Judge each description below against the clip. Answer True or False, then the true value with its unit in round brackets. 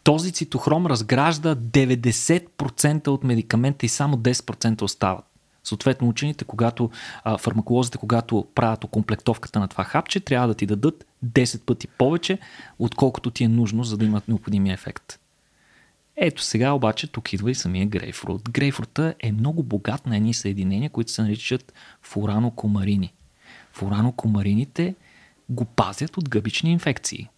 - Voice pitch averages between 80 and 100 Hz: False (120 Hz)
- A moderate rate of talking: True (135 wpm)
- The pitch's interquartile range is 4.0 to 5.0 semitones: True (4.5 semitones)